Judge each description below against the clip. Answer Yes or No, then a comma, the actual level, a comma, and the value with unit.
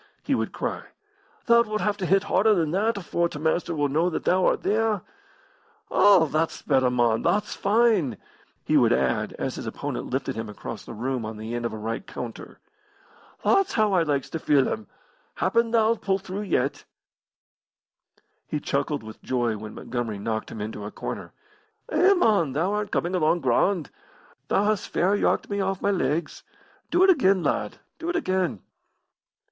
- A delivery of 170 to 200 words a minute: Yes, average, 180 wpm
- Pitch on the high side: No, medium, 170 Hz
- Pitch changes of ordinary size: No, wide, 8.5 semitones